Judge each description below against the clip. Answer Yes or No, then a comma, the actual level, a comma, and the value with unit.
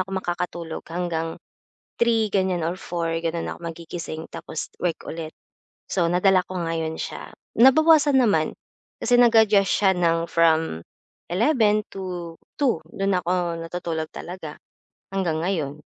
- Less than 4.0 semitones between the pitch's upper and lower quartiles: Yes, average, 3.1 semitones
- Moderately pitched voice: Yes, medium, 175 Hz